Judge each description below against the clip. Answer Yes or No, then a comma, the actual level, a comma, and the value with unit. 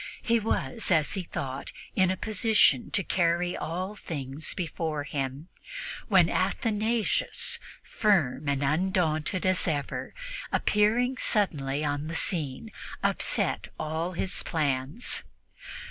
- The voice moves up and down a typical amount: No, wide, 5.9 semitones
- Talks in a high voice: No, medium, 170 Hz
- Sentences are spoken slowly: Yes, slow, 115 wpm